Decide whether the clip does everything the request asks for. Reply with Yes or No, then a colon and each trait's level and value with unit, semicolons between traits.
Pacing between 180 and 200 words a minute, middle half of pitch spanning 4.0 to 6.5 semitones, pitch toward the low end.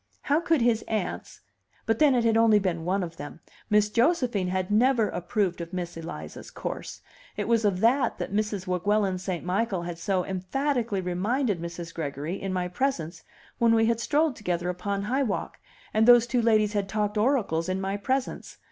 No: average, 185 wpm; average, 4.4 semitones; high, 205 Hz